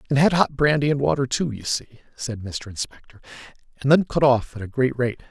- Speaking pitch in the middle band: No, low, 130 Hz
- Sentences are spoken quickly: Yes, fast, 225 wpm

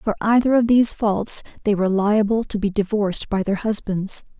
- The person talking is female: Yes, female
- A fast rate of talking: No, average, 190 wpm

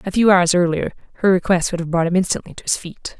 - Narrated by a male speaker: No, female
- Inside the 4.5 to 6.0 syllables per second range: No, 6.6 syllables/s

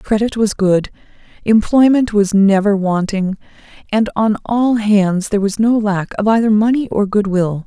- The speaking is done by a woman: Yes, female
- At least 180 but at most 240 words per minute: No, average, 165 wpm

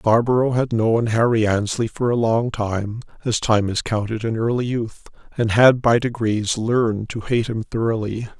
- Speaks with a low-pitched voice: Yes, low, 115 Hz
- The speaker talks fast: No, average, 180 wpm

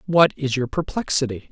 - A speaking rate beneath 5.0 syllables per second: No, 5.2 syllables/s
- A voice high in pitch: No, medium, 140 Hz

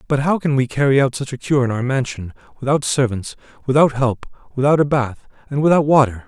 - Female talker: No, male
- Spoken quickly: Yes, fast, 210 wpm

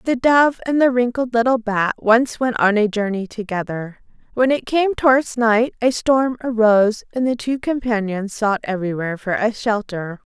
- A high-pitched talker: Yes, high, 230 Hz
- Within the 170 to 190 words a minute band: Yes, average, 175 wpm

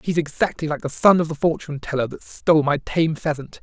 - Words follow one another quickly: Yes, fast, 230 wpm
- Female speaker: No, male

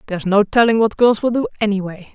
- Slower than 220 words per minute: No, fast, 225 wpm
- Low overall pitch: No, high, 215 Hz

